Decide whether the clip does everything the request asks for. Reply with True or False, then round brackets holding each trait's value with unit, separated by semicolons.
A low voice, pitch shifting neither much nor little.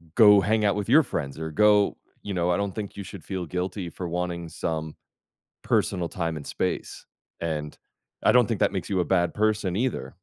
True (95 Hz; 3.5 semitones)